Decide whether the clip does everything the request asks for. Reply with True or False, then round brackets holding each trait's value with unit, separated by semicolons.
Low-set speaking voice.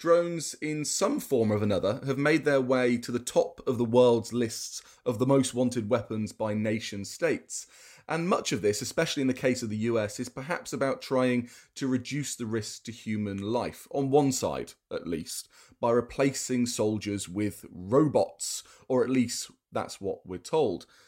True (125 Hz)